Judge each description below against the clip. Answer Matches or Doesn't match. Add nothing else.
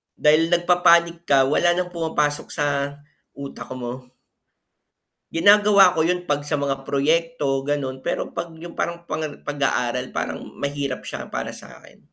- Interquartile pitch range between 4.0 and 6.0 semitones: Doesn't match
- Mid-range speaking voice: Matches